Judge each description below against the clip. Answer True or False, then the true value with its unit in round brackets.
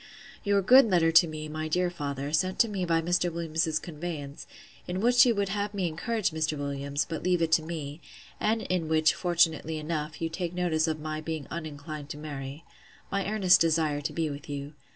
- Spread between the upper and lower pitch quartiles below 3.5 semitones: True (2.7 semitones)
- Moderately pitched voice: True (160 Hz)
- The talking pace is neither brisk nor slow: True (195 wpm)